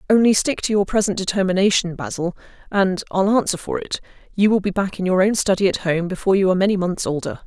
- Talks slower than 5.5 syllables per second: No, 6.5 syllables/s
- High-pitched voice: Yes, high, 195 Hz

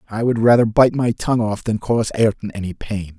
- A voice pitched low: Yes, low, 110 Hz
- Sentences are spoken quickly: Yes, fast, 225 wpm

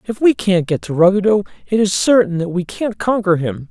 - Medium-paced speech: No, fast, 225 wpm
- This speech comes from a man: Yes, male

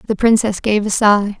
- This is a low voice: No, high, 210 Hz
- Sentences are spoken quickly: Yes, fast, 215 wpm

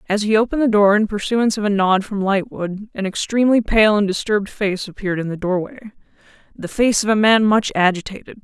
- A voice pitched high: Yes, high, 205 Hz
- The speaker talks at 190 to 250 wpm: Yes, average, 200 wpm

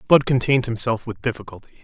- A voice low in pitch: Yes, low, 120 Hz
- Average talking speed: Yes, average, 165 wpm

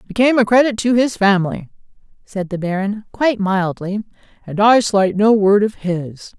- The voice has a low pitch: No, high, 205 Hz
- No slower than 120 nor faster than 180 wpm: Yes, average, 170 wpm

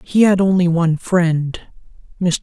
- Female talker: No, male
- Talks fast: No, slow, 125 wpm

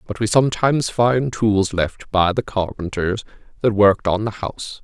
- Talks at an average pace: Yes, average, 175 wpm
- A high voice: No, low, 105 Hz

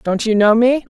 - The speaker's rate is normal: No, fast, 250 wpm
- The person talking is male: No, female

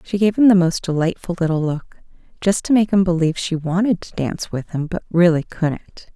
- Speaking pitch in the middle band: Yes, medium, 175 Hz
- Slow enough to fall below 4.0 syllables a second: No, 5.4 syllables/s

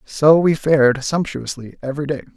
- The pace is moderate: Yes, average, 155 wpm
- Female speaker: No, male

